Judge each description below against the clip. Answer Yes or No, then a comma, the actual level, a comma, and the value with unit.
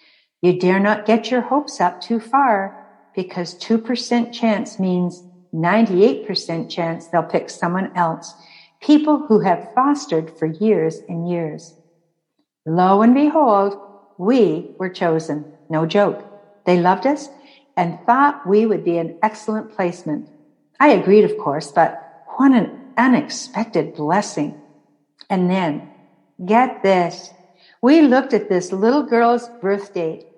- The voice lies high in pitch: Yes, high, 195 Hz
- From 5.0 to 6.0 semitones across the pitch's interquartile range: Yes, average, 5.3 semitones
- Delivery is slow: Yes, slow, 130 wpm